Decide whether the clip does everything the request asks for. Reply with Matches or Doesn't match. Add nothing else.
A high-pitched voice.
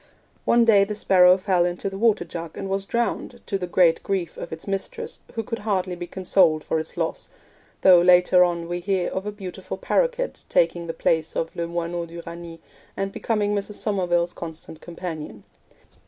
Doesn't match